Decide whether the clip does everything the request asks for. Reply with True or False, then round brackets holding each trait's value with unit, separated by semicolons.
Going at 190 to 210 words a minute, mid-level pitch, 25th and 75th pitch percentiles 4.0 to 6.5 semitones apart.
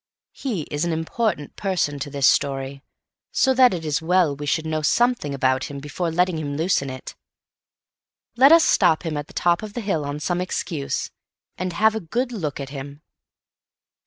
True (195 wpm; 160 Hz; 5.0 semitones)